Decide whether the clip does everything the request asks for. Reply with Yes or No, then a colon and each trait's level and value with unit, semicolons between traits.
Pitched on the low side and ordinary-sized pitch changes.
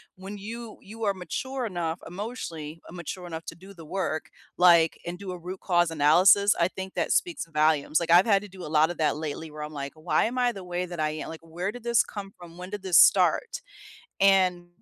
No: medium, 180 Hz; average, 3.4 semitones